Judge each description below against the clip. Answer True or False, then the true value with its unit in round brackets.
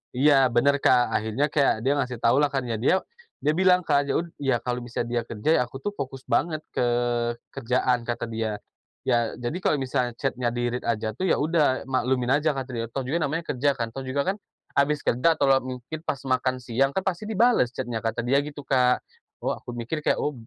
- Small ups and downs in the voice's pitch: False (3.2 semitones)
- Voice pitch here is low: True (130 Hz)